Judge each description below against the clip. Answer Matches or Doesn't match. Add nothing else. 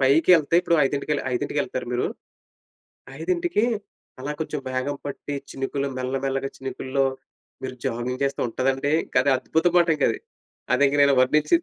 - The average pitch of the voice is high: Doesn't match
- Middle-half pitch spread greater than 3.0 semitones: Doesn't match